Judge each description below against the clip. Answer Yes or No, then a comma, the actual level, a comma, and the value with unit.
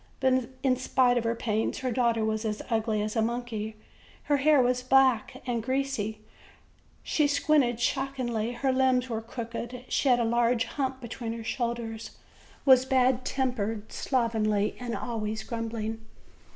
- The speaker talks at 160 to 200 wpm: No, average, 150 wpm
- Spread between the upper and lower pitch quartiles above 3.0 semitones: No, narrow, 2.5 semitones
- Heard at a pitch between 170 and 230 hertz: No, high, 240 Hz